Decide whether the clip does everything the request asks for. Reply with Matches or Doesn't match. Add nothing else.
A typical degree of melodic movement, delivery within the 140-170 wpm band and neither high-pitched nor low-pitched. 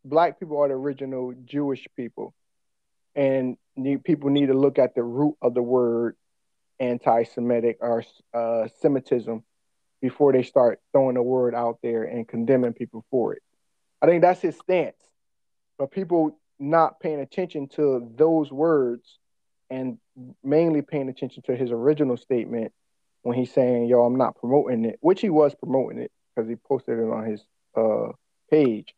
Doesn't match